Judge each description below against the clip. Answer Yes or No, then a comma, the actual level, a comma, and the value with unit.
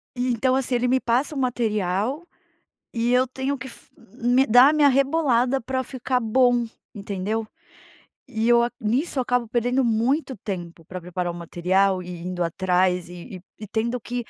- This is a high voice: Yes, high, 235 Hz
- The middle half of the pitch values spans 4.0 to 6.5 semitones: Yes, average, 5.1 semitones